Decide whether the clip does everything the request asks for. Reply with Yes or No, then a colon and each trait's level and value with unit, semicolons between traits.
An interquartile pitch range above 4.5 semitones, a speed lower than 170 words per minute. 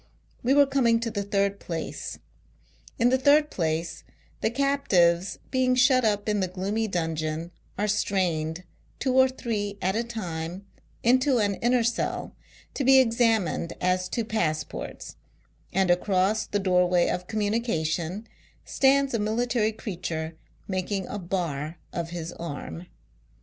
Yes: average, 5.2 semitones; average, 140 wpm